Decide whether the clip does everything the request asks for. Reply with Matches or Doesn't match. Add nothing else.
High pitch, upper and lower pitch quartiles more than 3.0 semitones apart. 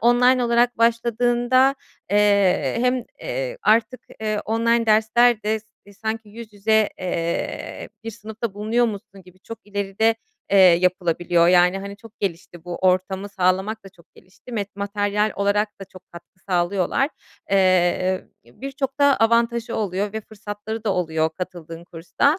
Matches